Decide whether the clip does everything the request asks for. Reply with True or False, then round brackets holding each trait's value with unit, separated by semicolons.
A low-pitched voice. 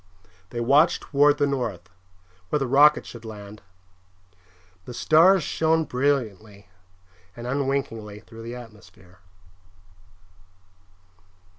True (125 Hz)